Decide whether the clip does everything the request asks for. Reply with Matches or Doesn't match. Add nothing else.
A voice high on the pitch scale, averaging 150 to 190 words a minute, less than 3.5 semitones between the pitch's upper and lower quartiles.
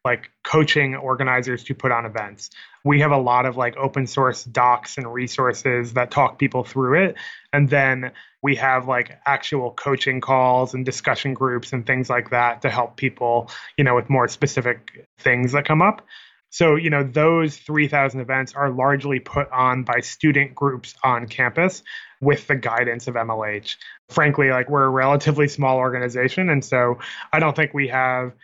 Doesn't match